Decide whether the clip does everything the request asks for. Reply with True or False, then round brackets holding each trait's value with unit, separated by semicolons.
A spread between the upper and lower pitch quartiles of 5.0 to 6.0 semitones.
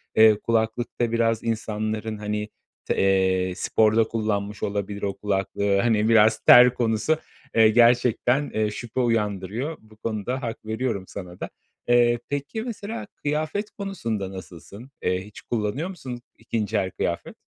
False (2.8 semitones)